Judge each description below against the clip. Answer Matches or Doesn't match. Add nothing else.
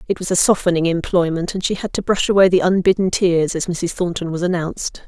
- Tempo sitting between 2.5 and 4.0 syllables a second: Doesn't match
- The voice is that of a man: Doesn't match